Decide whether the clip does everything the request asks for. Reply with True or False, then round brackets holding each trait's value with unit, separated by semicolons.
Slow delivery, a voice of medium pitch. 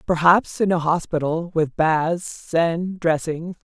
True (130 wpm; 165 Hz)